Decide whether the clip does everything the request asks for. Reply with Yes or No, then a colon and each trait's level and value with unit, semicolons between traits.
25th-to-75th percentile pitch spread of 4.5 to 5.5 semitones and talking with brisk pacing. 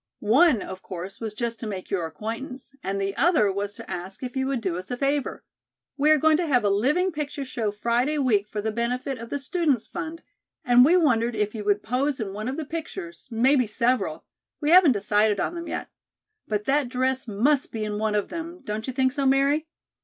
Yes: average, 5.2 semitones; fast, 220 wpm